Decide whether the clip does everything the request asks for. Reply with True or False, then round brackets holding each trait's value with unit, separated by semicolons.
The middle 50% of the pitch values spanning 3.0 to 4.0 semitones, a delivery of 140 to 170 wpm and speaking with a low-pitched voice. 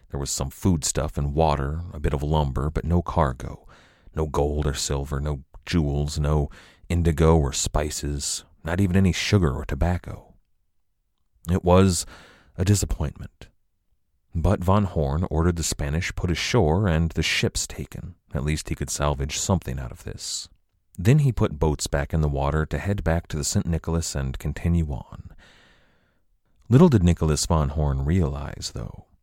True (3.4 semitones; 160 wpm; 80 Hz)